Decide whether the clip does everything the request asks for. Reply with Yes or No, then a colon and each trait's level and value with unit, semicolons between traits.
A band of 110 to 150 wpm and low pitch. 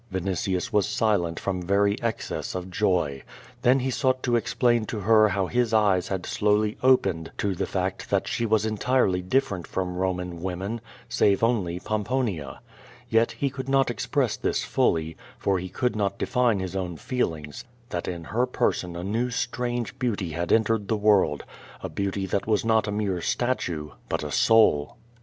No: average, 175 wpm; low, 100 Hz